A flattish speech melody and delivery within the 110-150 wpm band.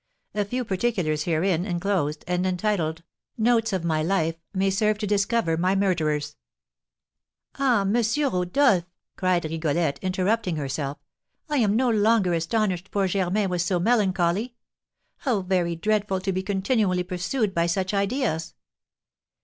No: average, 3.7 semitones; slow, 135 wpm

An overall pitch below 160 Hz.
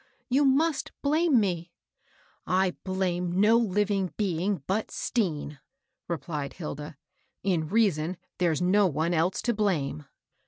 No: medium, 185 Hz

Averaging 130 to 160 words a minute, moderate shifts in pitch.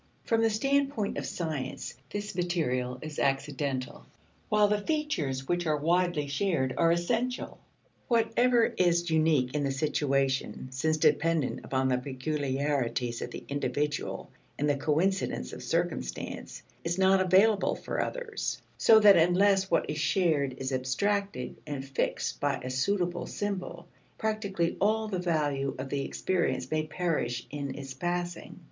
No: average, 140 wpm; wide, 6.0 semitones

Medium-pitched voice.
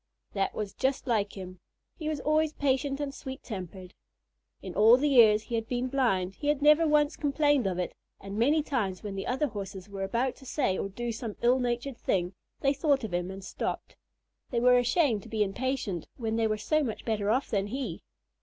No: high, 235 Hz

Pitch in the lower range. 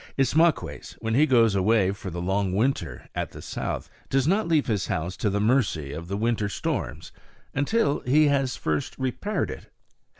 Yes: low, 115 Hz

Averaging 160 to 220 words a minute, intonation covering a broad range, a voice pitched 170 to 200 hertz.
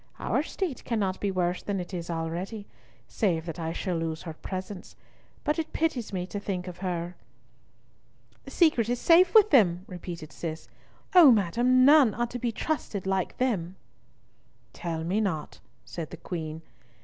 Yes: average, 165 wpm; wide, 5.9 semitones; high, 190 Hz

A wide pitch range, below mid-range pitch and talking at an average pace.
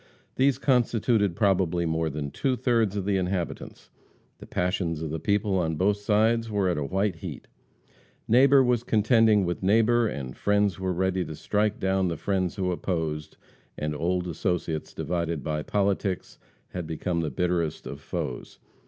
No: average, 4.0 semitones; very low, 95 Hz; average, 160 wpm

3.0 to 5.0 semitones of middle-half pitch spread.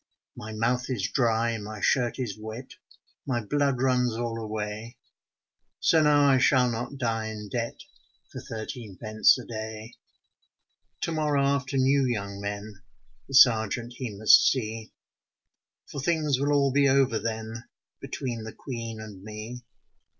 Yes: average, 3.3 semitones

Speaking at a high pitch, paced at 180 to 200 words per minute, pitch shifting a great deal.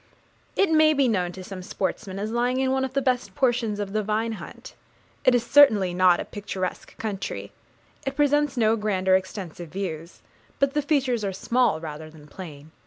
Yes: high, 215 Hz; average, 190 wpm; wide, 5.8 semitones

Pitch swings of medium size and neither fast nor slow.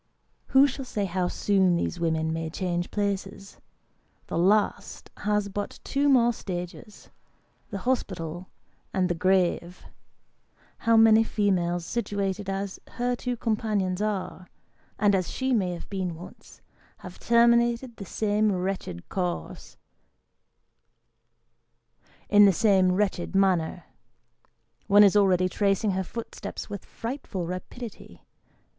No: average, 3.0 semitones; slow, 120 wpm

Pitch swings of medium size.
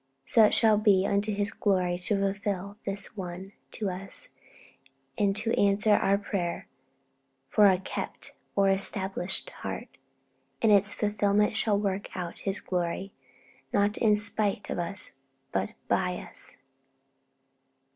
No: narrow, 1.7 semitones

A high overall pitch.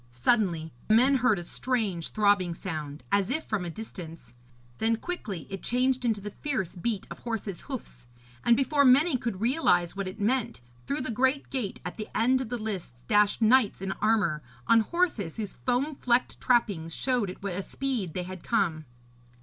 Yes: high, 215 Hz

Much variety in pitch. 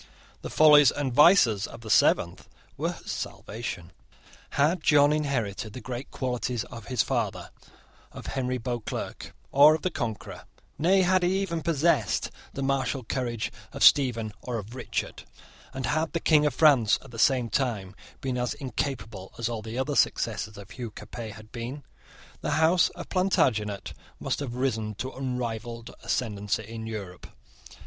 No: average, 4.4 semitones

